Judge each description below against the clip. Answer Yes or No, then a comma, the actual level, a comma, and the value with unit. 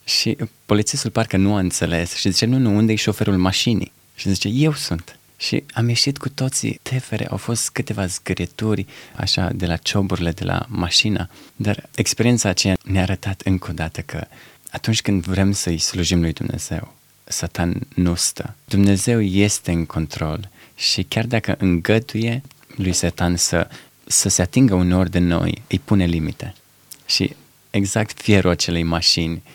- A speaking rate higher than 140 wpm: Yes, average, 160 wpm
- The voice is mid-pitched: No, low, 100 Hz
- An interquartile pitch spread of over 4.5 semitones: No, average, 4.2 semitones